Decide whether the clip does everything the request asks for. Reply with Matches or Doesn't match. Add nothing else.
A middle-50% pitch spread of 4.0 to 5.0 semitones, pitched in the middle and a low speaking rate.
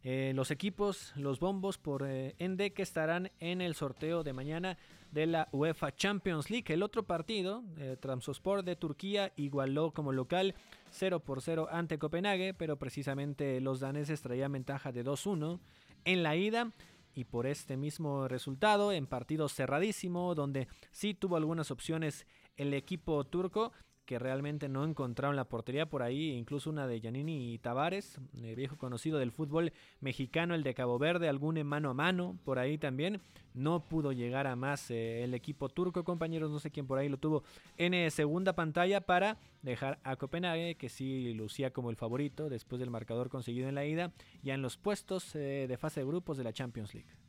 Doesn't match